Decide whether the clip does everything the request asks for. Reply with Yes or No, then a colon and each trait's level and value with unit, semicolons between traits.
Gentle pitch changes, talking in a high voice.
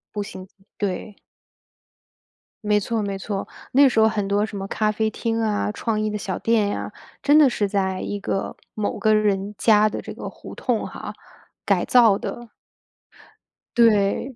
Yes: narrow, 2.0 semitones; high, 210 Hz